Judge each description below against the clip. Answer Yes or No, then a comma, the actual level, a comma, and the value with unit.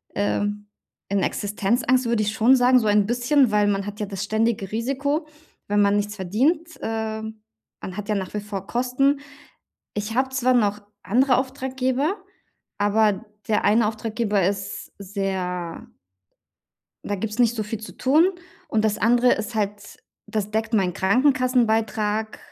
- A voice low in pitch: No, high, 220 Hz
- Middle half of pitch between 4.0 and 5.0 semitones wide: No, average, 3.2 semitones